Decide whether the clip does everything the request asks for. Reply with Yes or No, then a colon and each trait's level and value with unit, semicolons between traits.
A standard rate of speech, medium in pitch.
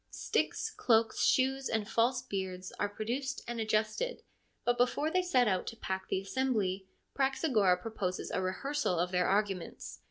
No: average, 155 wpm; high, 220 Hz